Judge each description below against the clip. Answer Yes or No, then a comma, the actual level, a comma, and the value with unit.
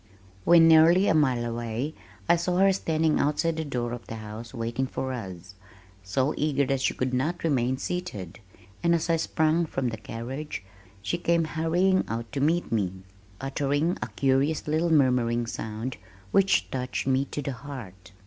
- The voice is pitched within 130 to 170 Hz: Yes, low, 135 Hz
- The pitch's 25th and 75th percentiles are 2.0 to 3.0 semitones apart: No, average, 5.3 semitones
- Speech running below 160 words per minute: No, average, 170 wpm